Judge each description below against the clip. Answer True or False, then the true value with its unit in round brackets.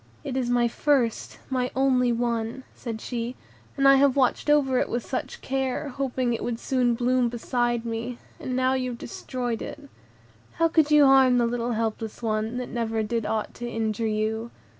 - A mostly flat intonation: True (2.2 semitones)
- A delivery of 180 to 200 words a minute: True (185 wpm)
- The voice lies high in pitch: True (245 Hz)